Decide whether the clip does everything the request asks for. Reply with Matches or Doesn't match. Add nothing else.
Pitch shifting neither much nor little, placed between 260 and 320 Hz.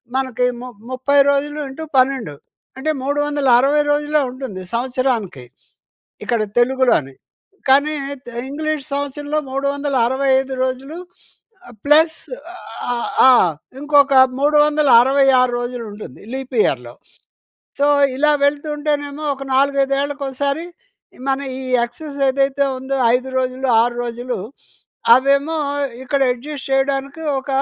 Doesn't match